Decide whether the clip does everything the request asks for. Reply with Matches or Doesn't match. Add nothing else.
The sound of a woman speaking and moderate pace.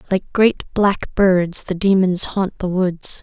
Matches